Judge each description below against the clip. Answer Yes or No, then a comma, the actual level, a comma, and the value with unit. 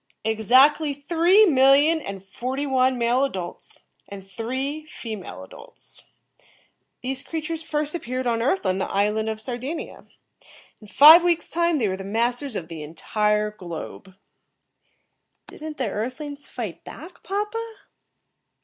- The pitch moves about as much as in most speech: No, wide, 6.3 semitones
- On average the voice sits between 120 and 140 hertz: No, very high, 255 Hz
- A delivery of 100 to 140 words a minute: Yes, slow, 135 wpm